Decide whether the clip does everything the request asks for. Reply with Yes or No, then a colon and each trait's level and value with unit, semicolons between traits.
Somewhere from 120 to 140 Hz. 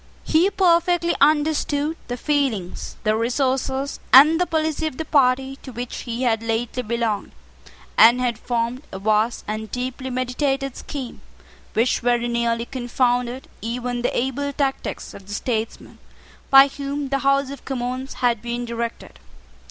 No: very high, 250 Hz